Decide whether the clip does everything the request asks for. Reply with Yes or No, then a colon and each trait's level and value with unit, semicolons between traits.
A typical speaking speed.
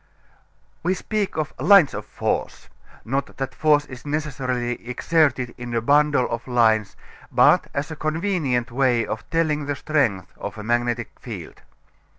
Yes: average, 150 wpm